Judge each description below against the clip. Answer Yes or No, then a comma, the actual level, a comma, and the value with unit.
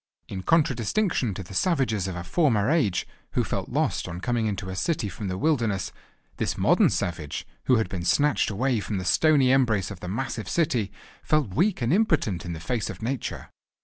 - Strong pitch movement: Yes, wide, 6.6 semitones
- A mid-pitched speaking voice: No, low, 110 Hz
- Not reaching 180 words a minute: No, average, 195 wpm